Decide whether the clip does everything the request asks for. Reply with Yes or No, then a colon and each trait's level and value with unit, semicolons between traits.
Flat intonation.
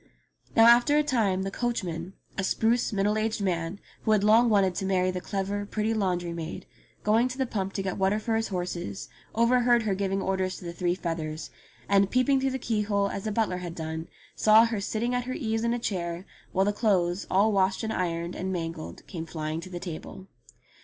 No: average, 3.8 semitones